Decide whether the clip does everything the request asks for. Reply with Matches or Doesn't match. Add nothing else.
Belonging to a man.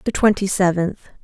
Doesn't match